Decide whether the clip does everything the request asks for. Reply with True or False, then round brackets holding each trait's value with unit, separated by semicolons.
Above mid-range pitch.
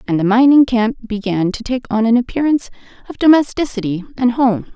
True (235 Hz)